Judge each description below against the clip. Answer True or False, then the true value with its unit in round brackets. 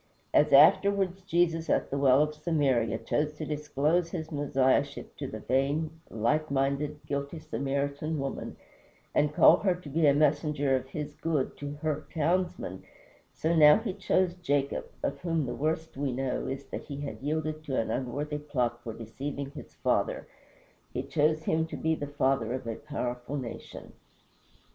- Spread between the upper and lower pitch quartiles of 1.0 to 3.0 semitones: True (2.7 semitones)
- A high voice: False (145 Hz)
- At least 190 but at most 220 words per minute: False (165 wpm)